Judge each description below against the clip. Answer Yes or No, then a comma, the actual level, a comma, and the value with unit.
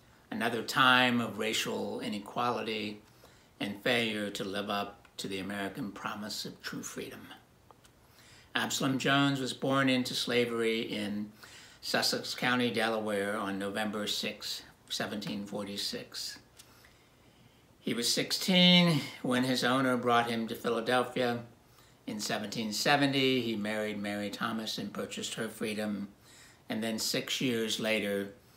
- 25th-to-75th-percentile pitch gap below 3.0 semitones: No, average, 3.3 semitones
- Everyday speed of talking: No, slow, 120 wpm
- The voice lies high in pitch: No, low, 115 Hz